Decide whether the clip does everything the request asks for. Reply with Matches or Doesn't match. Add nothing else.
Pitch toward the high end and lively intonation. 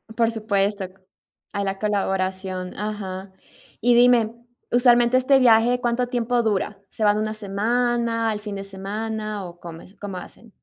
Doesn't match